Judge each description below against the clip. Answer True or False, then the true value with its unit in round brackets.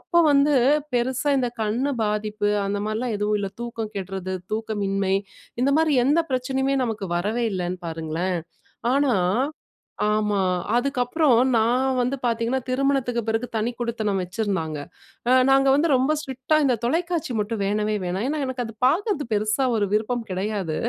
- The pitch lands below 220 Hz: False (230 Hz)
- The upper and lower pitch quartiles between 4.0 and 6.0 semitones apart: True (4.3 semitones)